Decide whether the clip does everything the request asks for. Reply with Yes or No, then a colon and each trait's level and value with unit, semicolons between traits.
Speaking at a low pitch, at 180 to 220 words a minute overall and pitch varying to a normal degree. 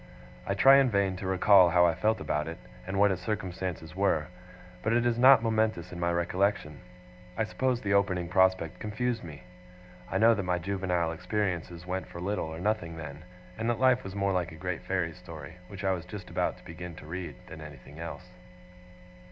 Yes: very low, 90 Hz; average, 200 wpm; average, 3.4 semitones